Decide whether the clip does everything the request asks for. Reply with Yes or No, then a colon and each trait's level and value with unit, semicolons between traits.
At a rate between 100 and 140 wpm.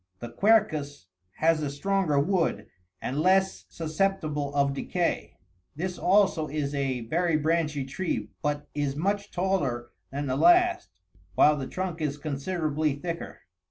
Yes: slow, 135 wpm